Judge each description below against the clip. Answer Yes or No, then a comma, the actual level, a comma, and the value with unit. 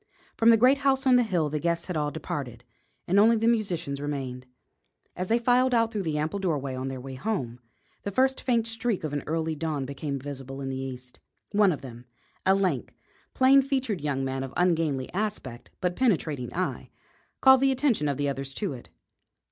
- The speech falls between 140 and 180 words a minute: No, average, 195 wpm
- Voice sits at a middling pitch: Yes, medium, 165 Hz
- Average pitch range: No, wide, 8.7 semitones